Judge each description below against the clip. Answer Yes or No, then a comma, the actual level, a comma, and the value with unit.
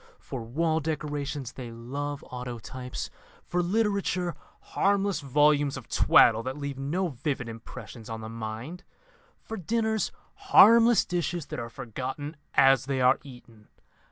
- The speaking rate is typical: No, slow, 130 wpm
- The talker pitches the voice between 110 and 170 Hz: Yes, medium, 140 Hz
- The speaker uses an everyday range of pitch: No, wide, 5.9 semitones